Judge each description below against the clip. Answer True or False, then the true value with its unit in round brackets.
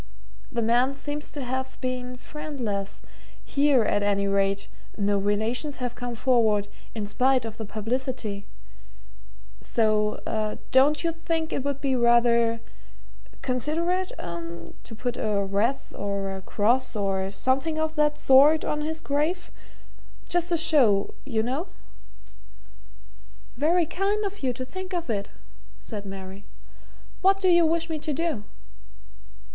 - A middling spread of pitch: False (6.3 semitones)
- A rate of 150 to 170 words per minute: False (140 wpm)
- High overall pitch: True (255 Hz)